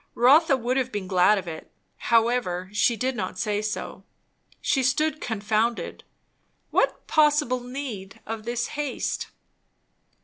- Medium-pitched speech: No, high, 240 Hz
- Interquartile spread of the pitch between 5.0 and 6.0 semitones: No, average, 3.8 semitones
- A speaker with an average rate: No, slow, 130 wpm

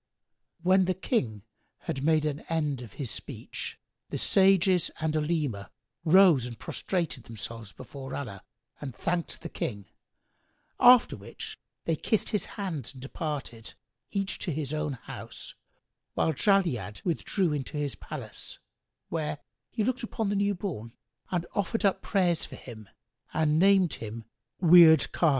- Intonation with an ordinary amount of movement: No, wide, 6.2 semitones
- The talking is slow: No, average, 145 wpm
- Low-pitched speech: No, medium, 155 Hz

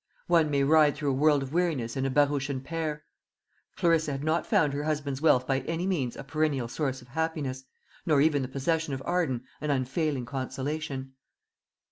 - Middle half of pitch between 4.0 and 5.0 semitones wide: No, average, 2.9 semitones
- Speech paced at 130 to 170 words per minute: No, average, 185 wpm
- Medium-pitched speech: Yes, medium, 145 Hz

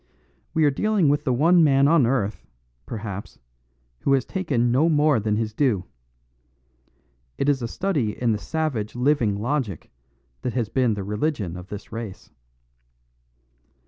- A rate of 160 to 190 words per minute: No, average, 150 wpm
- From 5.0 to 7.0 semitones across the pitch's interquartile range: Yes, wide, 5.6 semitones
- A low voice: Yes, low, 125 Hz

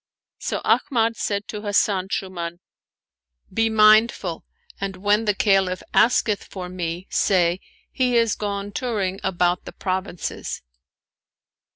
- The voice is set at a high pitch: Yes, high, 200 Hz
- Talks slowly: Yes, slow, 125 wpm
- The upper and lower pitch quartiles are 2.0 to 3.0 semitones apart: Yes, average, 2.7 semitones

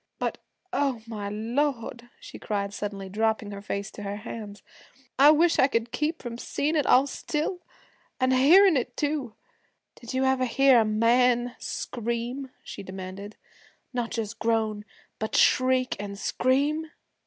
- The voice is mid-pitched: No, high, 235 Hz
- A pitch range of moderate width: Yes, average, 4.0 semitones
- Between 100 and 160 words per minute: Yes, average, 150 wpm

